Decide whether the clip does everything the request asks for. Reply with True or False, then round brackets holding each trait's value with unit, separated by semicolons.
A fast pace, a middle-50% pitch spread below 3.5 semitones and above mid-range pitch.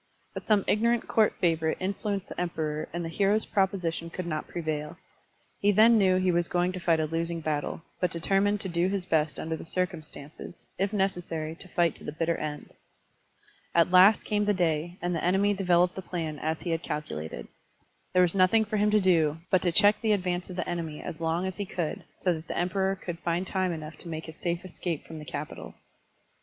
False (215 wpm; 2.9 semitones; 175 Hz)